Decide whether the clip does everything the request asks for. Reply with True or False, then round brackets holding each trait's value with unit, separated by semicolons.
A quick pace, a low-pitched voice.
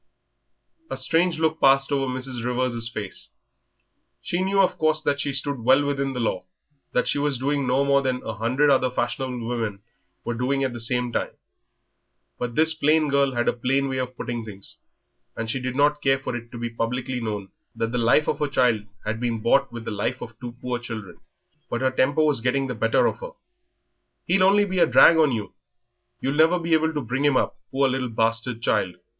True (210 wpm; 130 Hz)